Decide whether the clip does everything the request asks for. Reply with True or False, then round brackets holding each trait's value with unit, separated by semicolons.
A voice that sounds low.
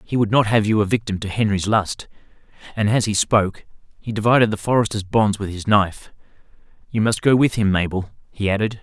True (105 Hz)